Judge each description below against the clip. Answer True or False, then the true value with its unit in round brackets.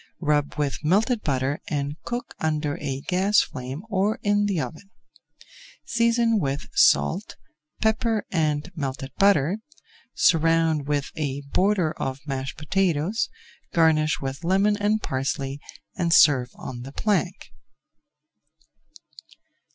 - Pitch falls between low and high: True (160 Hz)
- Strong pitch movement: True (6.1 semitones)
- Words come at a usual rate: False (115 wpm)